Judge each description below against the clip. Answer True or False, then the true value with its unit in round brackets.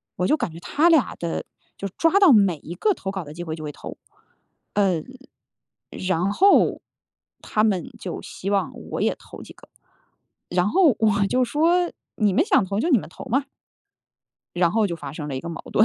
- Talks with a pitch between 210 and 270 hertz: False (200 Hz)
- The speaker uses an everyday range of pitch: False (7.7 semitones)